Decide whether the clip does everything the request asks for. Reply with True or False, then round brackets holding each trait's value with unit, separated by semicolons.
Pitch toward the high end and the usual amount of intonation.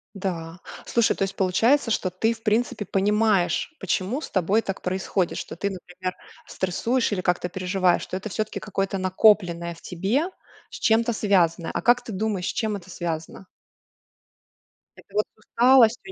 True (195 Hz; 3.4 semitones)